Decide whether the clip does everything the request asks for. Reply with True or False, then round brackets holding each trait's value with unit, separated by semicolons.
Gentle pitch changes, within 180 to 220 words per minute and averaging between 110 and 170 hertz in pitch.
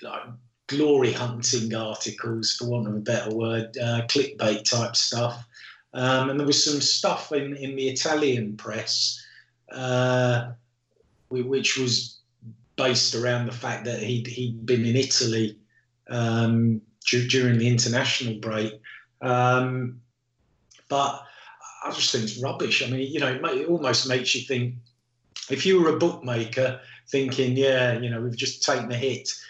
False (2.0 semitones; 155 wpm; 125 Hz)